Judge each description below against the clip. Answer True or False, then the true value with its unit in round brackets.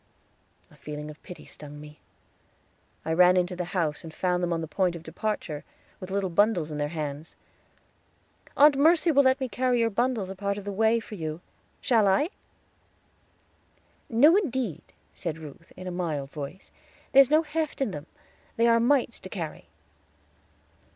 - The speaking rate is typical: True (170 wpm)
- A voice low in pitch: False (190 Hz)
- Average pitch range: False (6.7 semitones)